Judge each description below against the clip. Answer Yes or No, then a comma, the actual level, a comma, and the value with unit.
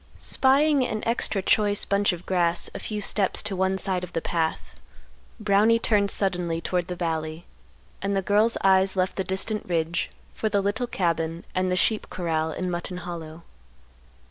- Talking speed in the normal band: Yes, average, 170 wpm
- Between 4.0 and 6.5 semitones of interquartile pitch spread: No, average, 3.0 semitones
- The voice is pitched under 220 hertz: Yes, high, 190 Hz